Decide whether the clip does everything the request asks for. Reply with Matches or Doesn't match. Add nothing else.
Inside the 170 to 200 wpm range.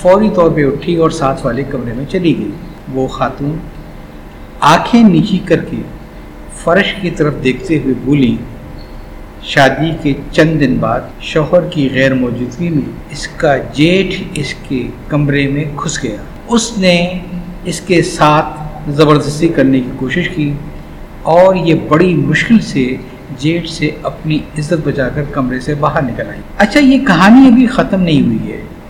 Doesn't match